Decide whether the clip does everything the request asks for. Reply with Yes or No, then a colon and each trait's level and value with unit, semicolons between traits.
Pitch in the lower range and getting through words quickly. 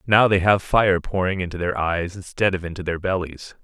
Yes: very low, 90 Hz; fast, 215 wpm